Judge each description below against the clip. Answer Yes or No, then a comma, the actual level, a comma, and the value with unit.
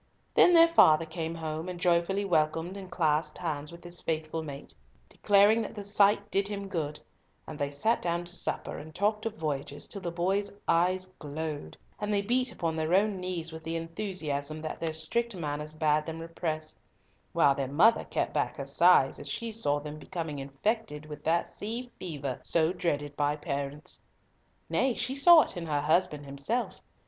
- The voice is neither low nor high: Yes, medium, 165 Hz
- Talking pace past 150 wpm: Yes, average, 185 wpm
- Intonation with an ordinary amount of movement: Yes, average, 4.6 semitones